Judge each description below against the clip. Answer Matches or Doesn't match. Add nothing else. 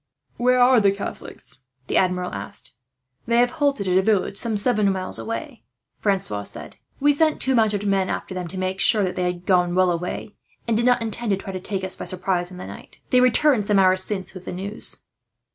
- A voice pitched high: Matches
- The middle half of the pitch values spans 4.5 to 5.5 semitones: Doesn't match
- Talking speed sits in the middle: Doesn't match